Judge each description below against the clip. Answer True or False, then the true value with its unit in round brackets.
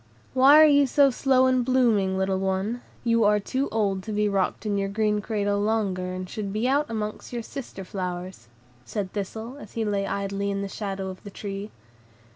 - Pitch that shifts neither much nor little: True (3.1 semitones)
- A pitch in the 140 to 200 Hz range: False (210 Hz)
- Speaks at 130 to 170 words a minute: False (200 wpm)